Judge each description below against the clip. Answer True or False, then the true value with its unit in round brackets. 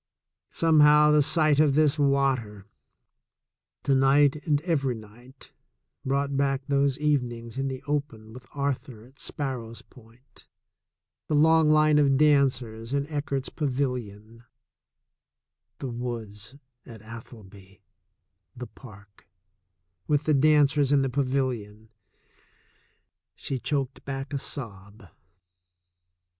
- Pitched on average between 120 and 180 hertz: True (135 Hz)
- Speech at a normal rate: False (115 wpm)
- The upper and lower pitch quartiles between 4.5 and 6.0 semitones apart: False (3.7 semitones)